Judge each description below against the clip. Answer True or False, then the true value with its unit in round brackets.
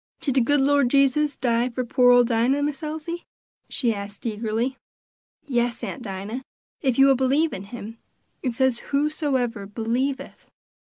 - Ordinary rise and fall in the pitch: True (3.3 semitones)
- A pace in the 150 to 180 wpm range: True (160 wpm)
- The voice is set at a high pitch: True (255 Hz)